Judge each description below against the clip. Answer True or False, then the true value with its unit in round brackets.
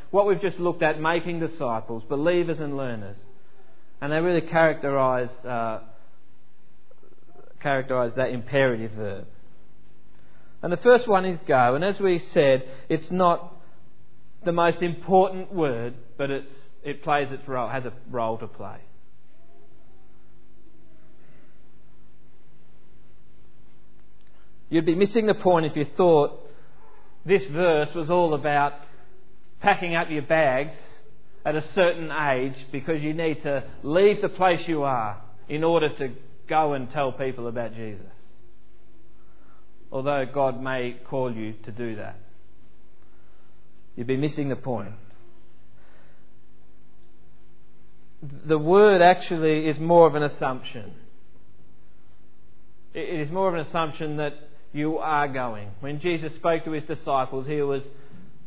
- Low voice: False (145 Hz)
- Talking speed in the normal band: False (125 wpm)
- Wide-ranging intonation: False (5.0 semitones)